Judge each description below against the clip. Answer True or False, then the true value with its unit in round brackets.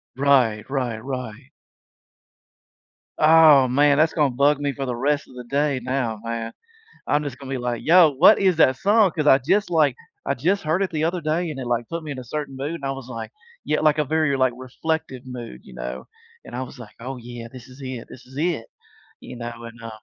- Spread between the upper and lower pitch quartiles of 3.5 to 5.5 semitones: True (3.9 semitones)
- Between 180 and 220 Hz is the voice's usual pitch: False (135 Hz)